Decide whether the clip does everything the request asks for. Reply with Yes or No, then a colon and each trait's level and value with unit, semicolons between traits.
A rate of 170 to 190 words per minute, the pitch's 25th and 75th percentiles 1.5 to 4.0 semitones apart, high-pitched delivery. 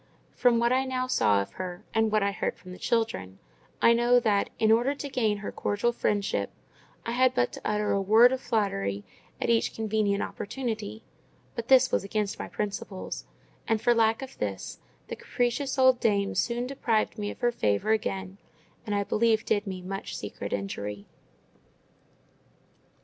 Yes: average, 175 wpm; average, 3.3 semitones; high, 215 Hz